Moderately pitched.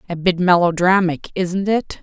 Yes: medium, 180 Hz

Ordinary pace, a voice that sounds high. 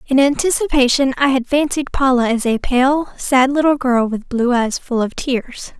Yes: average, 185 wpm; very high, 260 Hz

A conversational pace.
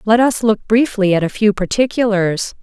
Yes: average, 185 wpm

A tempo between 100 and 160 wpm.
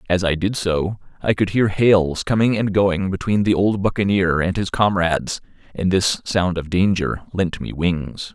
No: average, 185 wpm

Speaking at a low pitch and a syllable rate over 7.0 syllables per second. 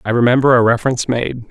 Yes: low, 120 Hz; 7.2 syllables/s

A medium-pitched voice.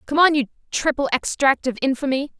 No: very high, 275 Hz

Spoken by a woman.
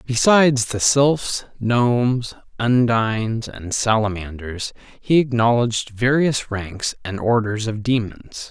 No: male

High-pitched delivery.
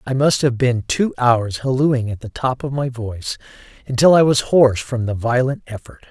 No: low, 125 Hz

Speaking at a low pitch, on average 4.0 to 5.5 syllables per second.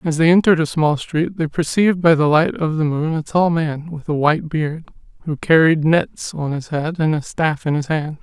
No: medium, 155 Hz; 5.1 syllables/s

